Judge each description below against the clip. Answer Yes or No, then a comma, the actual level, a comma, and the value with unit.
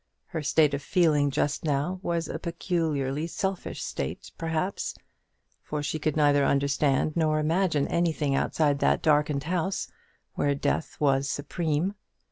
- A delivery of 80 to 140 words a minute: Yes, slow, 135 wpm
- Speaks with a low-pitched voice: No, medium, 155 Hz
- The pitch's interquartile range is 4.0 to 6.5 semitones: No, average, 2.8 semitones